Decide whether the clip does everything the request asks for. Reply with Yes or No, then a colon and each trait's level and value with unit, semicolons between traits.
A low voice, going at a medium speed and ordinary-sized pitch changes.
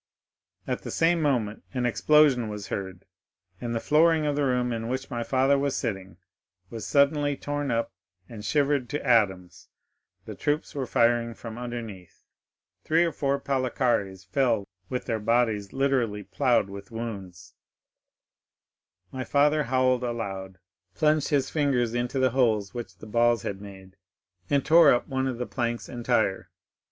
Yes: low, 120 Hz; average, 150 wpm; average, 4.3 semitones